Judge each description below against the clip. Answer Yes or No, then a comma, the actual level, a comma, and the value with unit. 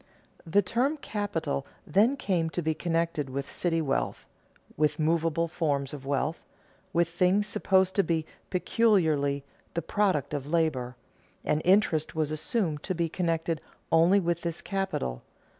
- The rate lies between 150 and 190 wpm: No, average, 140 wpm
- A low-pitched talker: No, medium, 165 Hz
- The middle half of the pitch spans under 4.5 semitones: Yes, average, 3.7 semitones